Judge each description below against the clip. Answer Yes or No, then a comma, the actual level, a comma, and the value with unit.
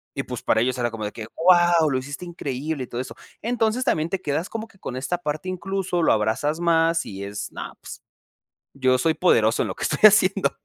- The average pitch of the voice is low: No, medium, 160 Hz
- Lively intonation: Yes, wide, 5.9 semitones